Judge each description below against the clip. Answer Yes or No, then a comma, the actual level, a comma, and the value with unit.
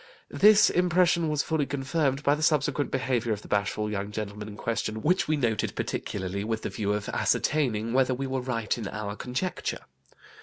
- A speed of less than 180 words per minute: No, average, 185 wpm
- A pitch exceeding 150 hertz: No, low, 125 Hz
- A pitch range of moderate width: No, wide, 5.7 semitones